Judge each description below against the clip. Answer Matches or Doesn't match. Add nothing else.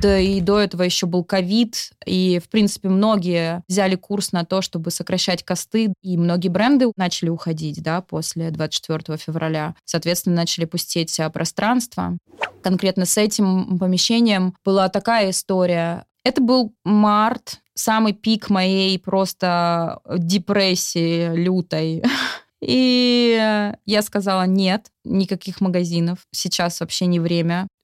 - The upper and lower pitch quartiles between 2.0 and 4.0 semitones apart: Matches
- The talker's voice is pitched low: Doesn't match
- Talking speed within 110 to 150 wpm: Matches